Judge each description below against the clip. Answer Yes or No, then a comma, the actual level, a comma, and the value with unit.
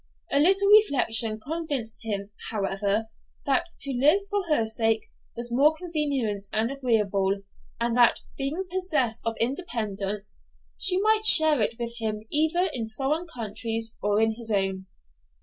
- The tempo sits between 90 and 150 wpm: Yes, average, 145 wpm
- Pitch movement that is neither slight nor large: No, wide, 6.1 semitones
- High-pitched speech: Yes, high, 235 Hz